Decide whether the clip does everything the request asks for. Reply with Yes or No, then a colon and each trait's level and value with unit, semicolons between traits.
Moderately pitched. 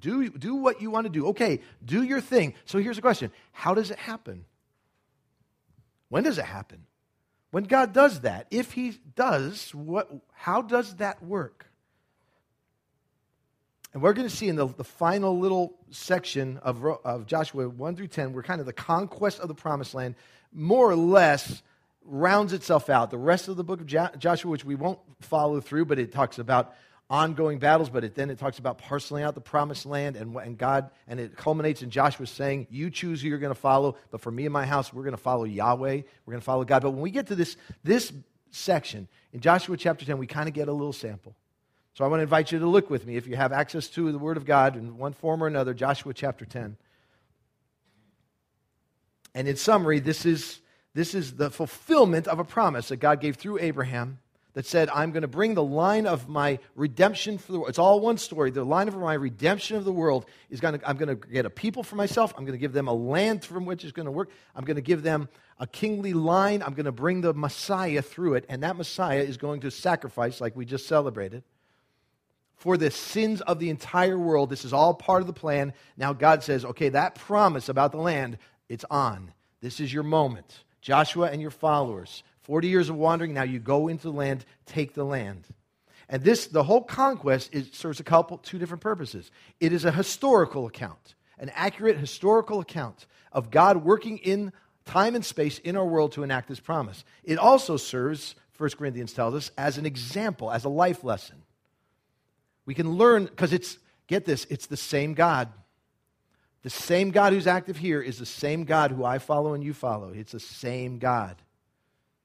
Yes: medium, 150 Hz